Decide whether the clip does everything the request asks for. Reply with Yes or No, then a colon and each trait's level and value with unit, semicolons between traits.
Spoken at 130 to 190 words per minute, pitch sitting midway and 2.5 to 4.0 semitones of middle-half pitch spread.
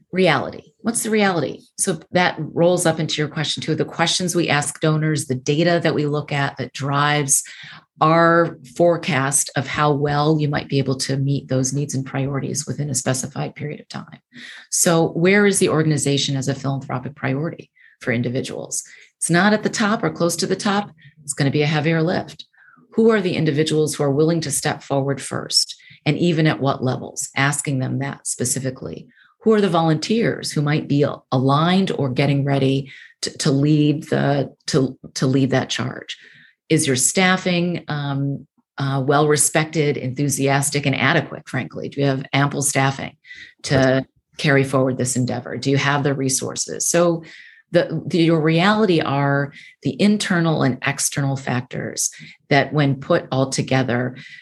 Yes: average, 170 wpm; medium, 145 Hz; average, 3.4 semitones